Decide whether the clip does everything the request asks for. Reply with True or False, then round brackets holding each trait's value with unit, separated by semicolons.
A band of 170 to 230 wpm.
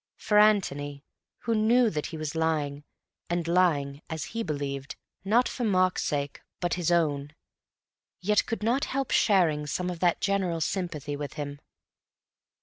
False (150 wpm)